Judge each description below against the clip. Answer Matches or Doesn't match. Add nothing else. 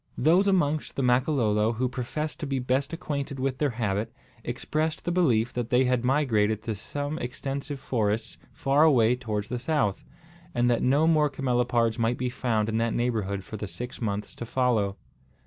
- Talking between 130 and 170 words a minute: Doesn't match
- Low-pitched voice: Matches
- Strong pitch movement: Doesn't match